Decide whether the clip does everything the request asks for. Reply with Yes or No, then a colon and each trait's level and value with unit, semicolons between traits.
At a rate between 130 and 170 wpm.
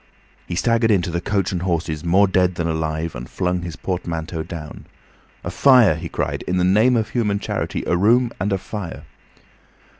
No: average, 185 wpm